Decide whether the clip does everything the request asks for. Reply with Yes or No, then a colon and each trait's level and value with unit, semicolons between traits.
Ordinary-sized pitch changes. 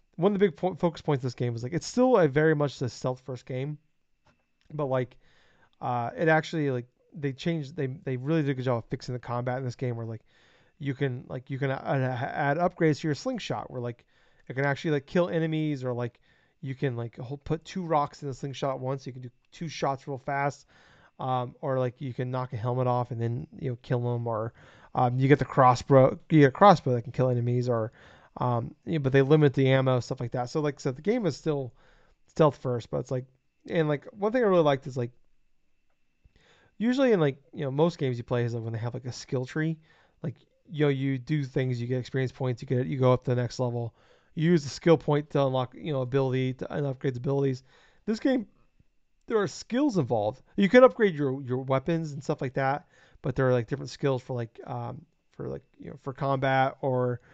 Yes: average, 3.4 semitones